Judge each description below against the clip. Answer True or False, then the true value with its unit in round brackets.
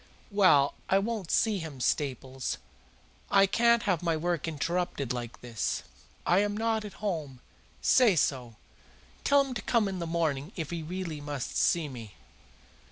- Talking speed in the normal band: True (160 wpm)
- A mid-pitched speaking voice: True (170 Hz)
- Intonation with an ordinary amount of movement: False (6.2 semitones)